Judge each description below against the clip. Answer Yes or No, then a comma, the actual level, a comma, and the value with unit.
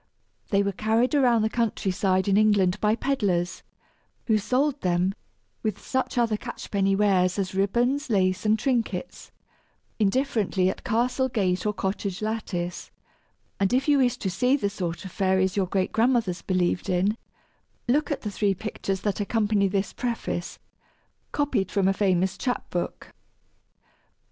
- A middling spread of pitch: Yes, average, 3.8 semitones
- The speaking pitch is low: No, high, 205 Hz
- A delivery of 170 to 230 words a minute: No, average, 155 wpm